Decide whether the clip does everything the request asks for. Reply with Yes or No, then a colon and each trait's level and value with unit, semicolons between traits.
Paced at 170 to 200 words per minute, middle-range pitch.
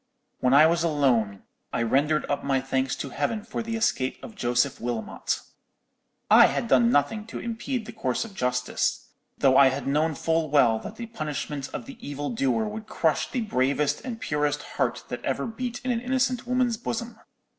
Yes: average, 190 wpm; medium, 150 Hz